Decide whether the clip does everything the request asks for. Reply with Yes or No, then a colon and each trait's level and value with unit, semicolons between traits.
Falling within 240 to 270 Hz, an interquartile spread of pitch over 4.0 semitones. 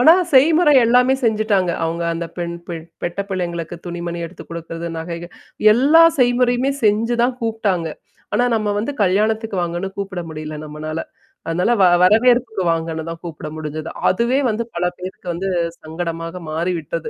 No: medium, 185 Hz; wide, 5.5 semitones